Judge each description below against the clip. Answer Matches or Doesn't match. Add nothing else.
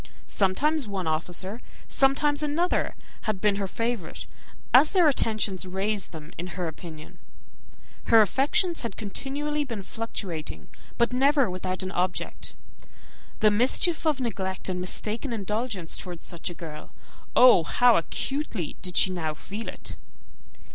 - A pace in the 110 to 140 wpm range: Matches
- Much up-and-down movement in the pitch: Matches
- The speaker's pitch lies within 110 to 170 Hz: Doesn't match